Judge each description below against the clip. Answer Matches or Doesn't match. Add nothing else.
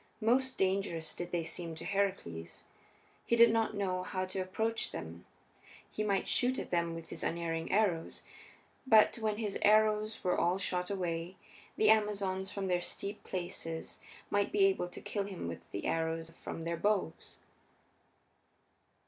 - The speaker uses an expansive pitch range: Doesn't match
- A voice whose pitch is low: Doesn't match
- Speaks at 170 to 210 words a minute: Doesn't match